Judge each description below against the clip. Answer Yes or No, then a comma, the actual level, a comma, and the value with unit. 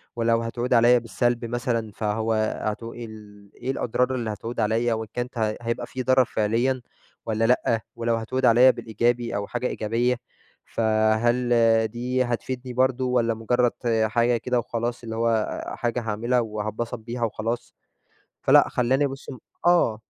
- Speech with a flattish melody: Yes, narrow, 1.7 semitones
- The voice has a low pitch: Yes, low, 120 Hz